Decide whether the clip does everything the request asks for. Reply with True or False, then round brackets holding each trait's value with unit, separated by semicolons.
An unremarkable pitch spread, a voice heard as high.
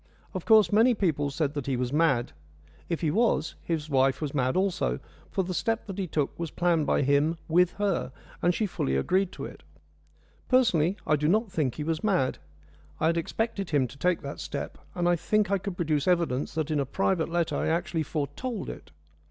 False (4.5 semitones; 165 Hz)